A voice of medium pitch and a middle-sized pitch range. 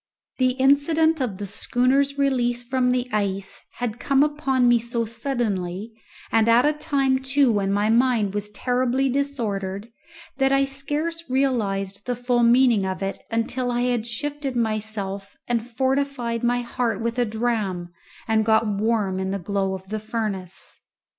No: high, 240 Hz; average, 4.1 semitones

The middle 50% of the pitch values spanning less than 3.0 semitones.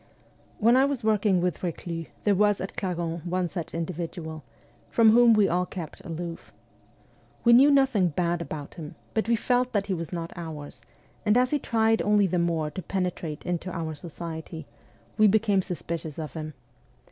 No: average, 4.4 semitones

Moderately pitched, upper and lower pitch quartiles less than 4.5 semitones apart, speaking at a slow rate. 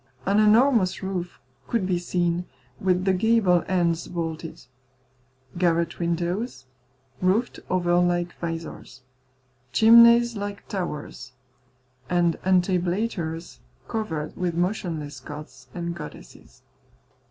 Yes: medium, 180 Hz; average, 2.8 semitones; slow, 95 wpm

